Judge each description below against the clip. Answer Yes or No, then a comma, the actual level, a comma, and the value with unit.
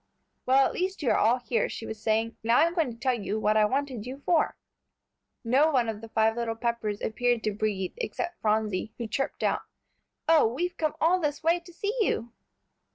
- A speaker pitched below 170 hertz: No, high, 240 Hz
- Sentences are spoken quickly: Yes, fast, 210 wpm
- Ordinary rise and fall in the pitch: No, wide, 5.9 semitones